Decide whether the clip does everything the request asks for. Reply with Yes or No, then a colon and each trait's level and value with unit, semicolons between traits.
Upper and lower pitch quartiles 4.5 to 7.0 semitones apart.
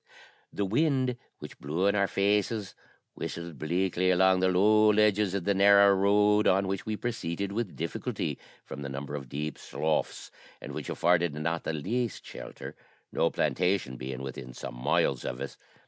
Yes: average, 4.9 semitones